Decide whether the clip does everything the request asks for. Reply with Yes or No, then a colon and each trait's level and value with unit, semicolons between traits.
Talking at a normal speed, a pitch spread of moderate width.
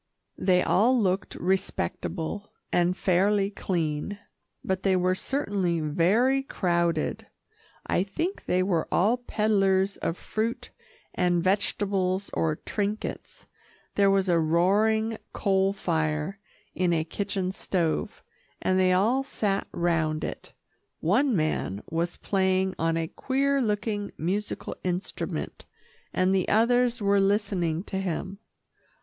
No: slow, 120 wpm; average, 3.0 semitones